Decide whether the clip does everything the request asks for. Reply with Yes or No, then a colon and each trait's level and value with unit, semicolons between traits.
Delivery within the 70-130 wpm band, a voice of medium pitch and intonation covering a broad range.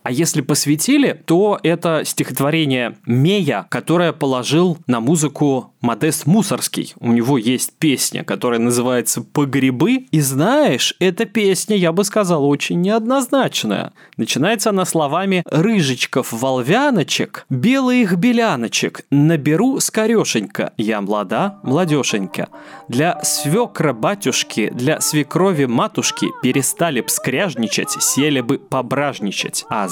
Yes: slow, 110 wpm; medium, 150 Hz; wide, 6.7 semitones